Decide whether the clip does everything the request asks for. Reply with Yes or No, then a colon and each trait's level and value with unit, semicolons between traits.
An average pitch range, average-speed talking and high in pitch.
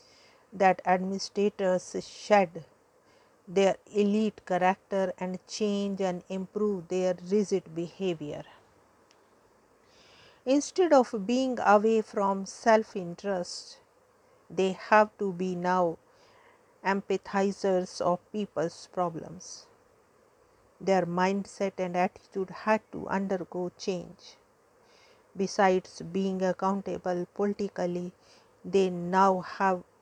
No: average, 4.3 semitones; slow, 90 wpm; high, 195 Hz